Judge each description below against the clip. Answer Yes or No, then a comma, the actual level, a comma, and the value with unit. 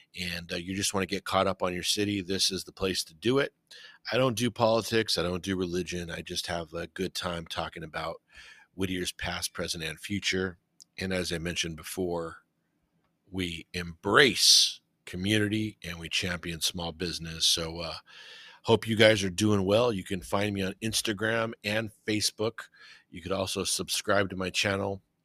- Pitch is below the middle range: Yes, very low, 95 Hz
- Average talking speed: Yes, average, 180 wpm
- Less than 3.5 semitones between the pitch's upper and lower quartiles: Yes, average, 2.9 semitones